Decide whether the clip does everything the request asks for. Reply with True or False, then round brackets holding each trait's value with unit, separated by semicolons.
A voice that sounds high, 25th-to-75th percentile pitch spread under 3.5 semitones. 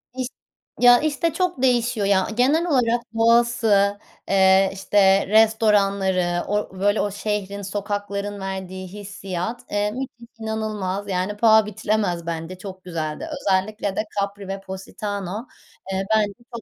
True (205 Hz; 2.6 semitones)